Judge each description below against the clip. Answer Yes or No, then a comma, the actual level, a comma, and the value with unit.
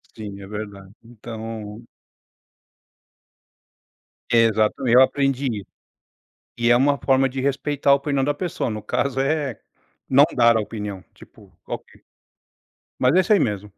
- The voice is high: No, low, 120 Hz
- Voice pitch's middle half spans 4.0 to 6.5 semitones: Yes, average, 4.3 semitones